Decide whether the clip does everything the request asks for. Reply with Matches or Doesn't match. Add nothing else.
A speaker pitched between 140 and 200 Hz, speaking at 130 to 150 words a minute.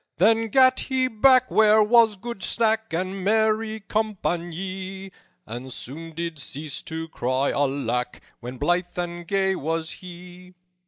Matches